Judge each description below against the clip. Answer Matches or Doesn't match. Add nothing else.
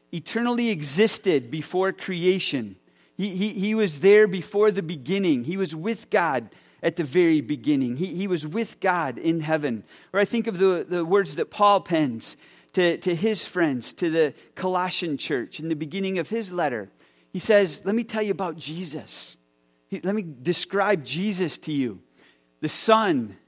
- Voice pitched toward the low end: Doesn't match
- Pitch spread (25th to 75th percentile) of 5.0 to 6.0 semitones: Doesn't match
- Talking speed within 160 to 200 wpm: Matches